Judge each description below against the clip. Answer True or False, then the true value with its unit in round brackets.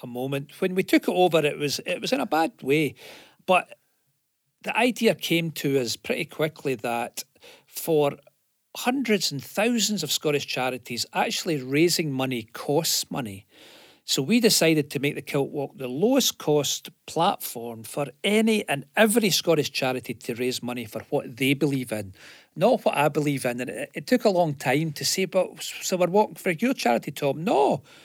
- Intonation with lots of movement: True (6.4 semitones)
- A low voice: False (145 Hz)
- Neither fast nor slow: True (180 wpm)